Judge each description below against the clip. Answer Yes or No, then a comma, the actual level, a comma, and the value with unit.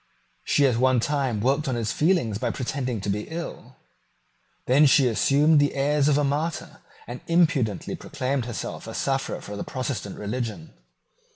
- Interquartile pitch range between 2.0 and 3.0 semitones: No, average, 3.8 semitones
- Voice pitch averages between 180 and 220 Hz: No, low, 135 Hz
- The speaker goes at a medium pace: Yes, average, 165 wpm